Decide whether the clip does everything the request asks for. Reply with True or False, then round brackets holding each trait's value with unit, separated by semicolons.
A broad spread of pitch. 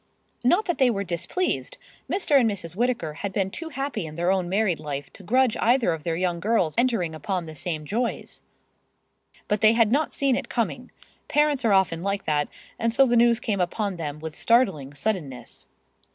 True (6.7 semitones)